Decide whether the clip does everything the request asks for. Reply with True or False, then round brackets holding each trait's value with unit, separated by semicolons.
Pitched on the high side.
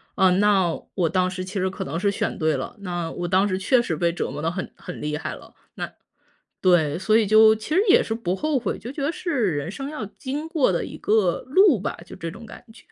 True (195 Hz)